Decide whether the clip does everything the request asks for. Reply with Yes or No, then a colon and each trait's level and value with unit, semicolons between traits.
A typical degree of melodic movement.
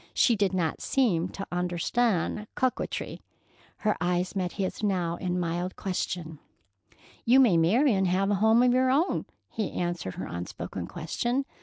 Yes: average, 4.5 semitones